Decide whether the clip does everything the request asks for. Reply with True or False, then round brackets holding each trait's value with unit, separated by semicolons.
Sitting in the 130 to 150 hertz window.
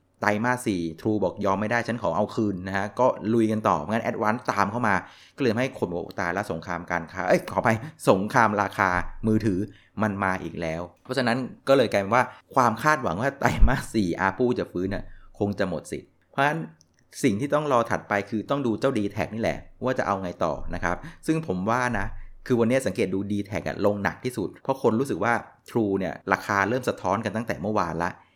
False (100 Hz)